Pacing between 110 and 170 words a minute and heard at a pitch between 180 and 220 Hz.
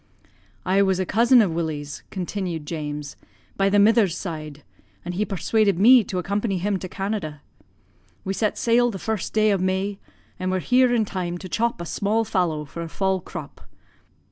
No: average, 180 wpm; high, 190 Hz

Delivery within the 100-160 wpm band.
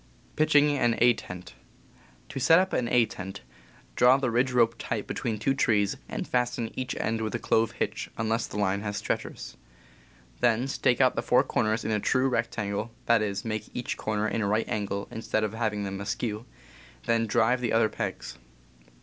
No: average, 185 wpm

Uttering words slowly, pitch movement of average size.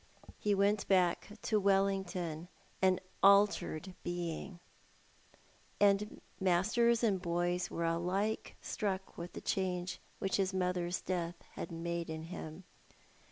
No: slow, 115 wpm; narrow, 2.3 semitones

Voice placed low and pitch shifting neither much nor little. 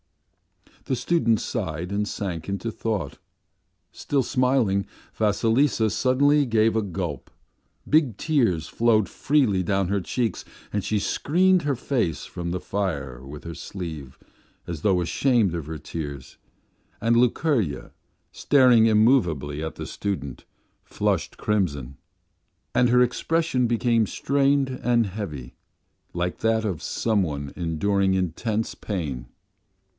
No: low, 105 Hz; wide, 6.5 semitones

